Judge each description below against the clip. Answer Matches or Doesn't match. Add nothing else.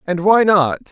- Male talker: Matches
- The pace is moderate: Matches